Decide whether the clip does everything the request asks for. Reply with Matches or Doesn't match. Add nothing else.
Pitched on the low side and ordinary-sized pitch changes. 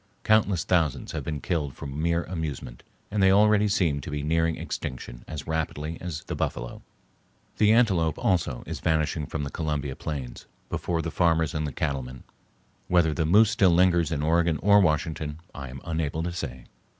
Matches